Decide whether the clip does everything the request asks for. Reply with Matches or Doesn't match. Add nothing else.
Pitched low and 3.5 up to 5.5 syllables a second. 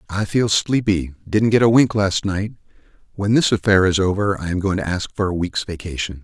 Matches